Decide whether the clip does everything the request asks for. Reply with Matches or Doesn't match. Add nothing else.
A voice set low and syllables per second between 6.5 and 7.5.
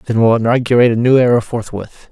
Matches